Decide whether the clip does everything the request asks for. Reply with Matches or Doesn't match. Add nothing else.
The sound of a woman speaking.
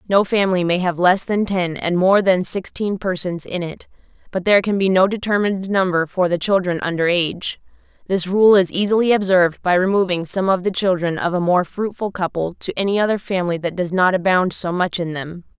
Matches